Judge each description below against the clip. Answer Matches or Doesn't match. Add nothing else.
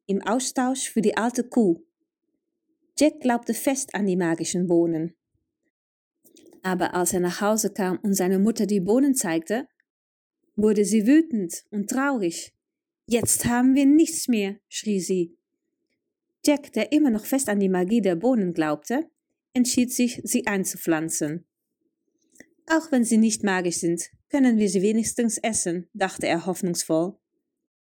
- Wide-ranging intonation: Matches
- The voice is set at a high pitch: Matches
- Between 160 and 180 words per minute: Doesn't match